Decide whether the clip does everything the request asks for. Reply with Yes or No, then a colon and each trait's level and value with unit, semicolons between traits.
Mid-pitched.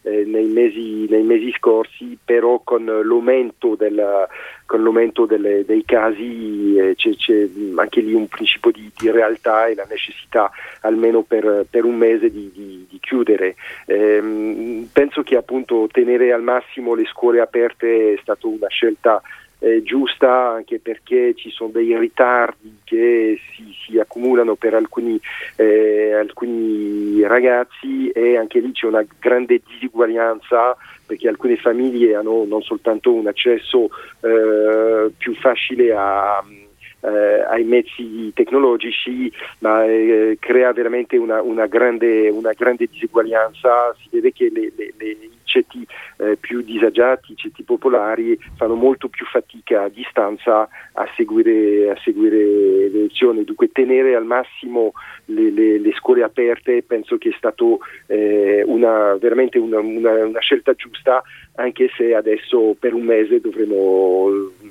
No: low, 120 Hz